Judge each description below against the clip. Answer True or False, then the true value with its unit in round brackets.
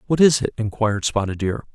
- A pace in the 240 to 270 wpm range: False (205 wpm)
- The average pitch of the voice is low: True (115 Hz)